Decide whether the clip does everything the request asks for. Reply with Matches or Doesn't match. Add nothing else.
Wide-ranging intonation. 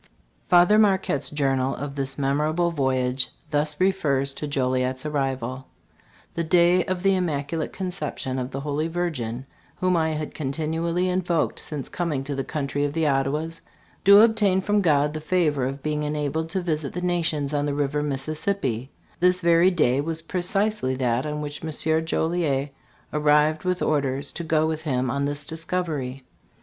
Doesn't match